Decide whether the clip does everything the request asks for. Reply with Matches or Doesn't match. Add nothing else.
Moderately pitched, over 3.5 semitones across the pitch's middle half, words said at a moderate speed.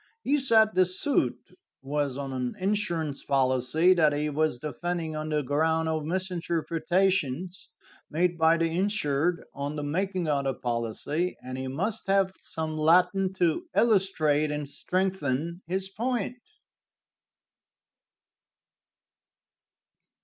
Doesn't match